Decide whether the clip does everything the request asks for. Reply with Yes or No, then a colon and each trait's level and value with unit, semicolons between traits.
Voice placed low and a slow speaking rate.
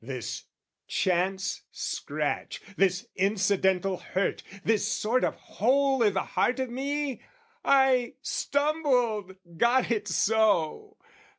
No: high, 220 Hz; slow, 105 wpm